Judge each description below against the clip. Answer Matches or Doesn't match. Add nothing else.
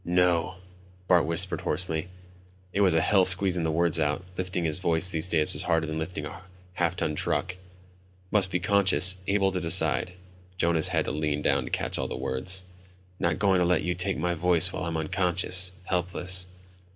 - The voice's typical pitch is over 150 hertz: Doesn't match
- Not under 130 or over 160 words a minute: Doesn't match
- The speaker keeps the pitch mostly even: Matches